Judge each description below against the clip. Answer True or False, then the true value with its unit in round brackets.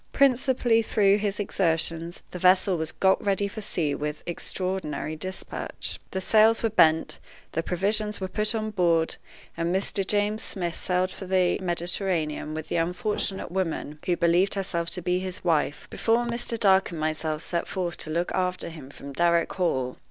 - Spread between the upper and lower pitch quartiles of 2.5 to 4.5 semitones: True (3.3 semitones)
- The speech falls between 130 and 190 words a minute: True (170 wpm)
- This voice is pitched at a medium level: True (180 Hz)